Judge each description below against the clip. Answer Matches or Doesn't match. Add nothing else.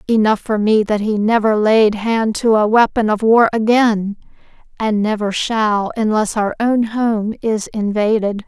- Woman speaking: Matches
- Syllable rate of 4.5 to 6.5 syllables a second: Doesn't match